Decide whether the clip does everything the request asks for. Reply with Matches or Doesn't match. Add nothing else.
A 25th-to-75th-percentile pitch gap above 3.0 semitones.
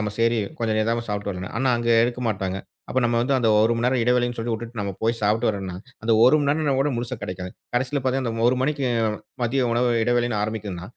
Doesn't match